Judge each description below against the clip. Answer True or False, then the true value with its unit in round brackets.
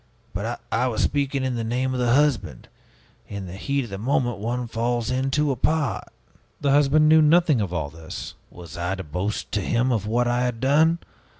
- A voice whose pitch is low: True (125 Hz)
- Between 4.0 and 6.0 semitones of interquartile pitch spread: True (4.8 semitones)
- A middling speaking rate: False (210 wpm)